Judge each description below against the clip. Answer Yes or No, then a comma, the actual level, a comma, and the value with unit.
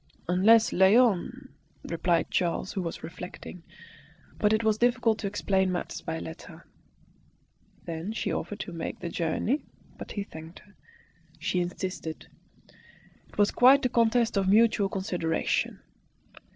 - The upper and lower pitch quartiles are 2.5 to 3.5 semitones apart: No, average, 4.1 semitones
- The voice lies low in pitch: No, high, 190 Hz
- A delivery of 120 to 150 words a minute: Yes, average, 140 wpm